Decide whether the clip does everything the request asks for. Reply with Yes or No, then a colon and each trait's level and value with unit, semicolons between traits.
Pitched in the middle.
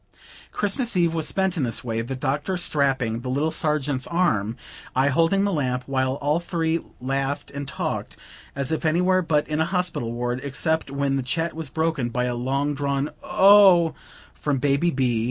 Yes: medium, 145 Hz